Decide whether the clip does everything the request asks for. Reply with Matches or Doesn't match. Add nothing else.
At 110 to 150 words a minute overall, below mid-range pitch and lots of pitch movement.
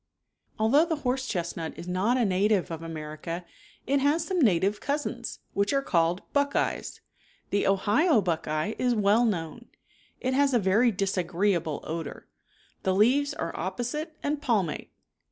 Doesn't match